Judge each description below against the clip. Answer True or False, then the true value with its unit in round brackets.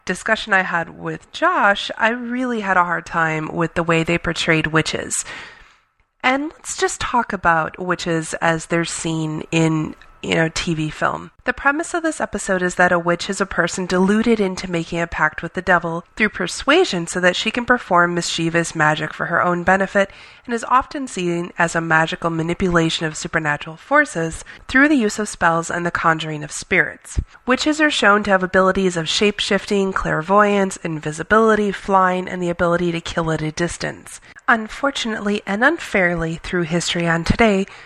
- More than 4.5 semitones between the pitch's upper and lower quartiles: False (4.0 semitones)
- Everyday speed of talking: True (180 wpm)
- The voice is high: False (180 Hz)